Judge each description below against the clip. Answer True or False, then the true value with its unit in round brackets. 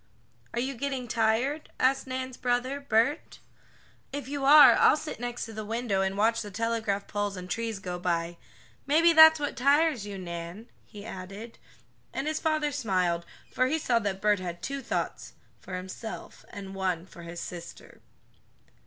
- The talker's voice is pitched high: True (225 Hz)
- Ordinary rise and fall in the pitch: False (6.0 semitones)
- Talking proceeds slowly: False (170 wpm)